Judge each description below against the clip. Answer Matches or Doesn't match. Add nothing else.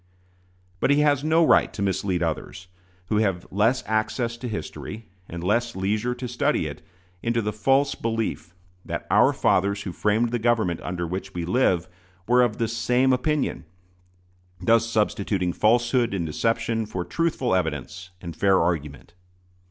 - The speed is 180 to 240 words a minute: Doesn't match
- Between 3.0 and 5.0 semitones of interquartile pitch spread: Matches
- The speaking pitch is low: Matches